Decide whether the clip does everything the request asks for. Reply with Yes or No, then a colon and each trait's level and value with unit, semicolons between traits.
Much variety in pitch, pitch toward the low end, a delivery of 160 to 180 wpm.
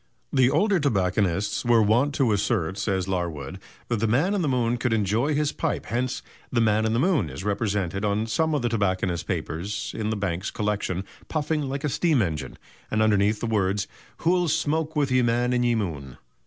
No: wide, 5.7 semitones; low, 110 Hz; average, 195 wpm